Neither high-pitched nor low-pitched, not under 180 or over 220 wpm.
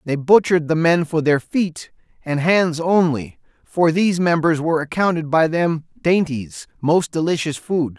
No: medium, 165 Hz; average, 160 wpm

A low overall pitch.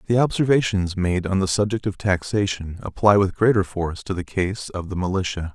Yes: very low, 95 Hz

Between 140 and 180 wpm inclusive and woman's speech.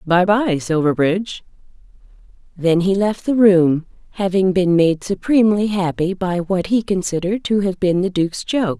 Yes: average, 155 wpm; female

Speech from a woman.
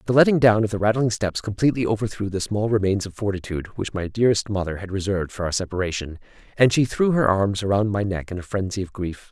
No: male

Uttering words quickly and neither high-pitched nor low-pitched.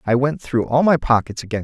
No: fast, 255 wpm; low, 125 Hz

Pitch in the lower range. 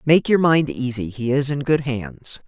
No: medium, 145 Hz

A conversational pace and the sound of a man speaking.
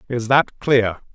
Yes: average, 155 wpm; male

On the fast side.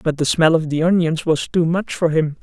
Yes: fast, 275 wpm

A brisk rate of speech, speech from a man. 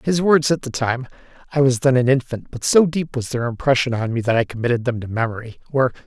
Yes: fast, 245 wpm; male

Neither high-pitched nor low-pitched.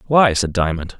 No: low, 100 Hz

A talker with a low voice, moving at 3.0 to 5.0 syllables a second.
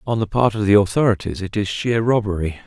No: low, 105 Hz; 6.0 syllables/s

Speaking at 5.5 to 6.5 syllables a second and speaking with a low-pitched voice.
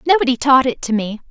No: 6.3 syllables/s; very high, 265 Hz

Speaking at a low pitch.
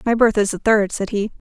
No: high, 210 Hz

